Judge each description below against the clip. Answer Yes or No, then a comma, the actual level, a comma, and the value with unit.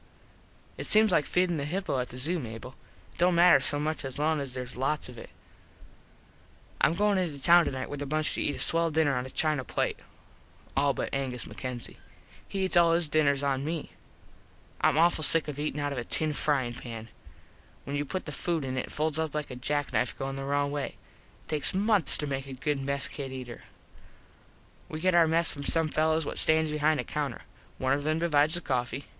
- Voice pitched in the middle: Yes, medium, 145 Hz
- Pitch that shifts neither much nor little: Yes, average, 3.0 semitones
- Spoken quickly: Yes, fast, 215 wpm